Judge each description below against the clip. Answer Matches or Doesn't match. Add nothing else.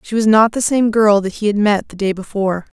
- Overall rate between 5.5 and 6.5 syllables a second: Matches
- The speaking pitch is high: Matches